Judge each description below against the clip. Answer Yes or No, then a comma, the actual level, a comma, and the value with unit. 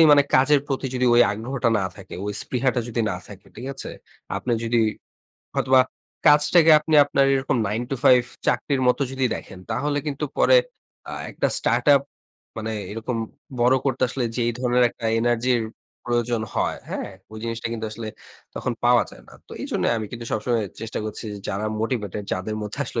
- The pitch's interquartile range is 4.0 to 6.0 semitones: No, average, 3.2 semitones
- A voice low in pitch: Yes, low, 120 Hz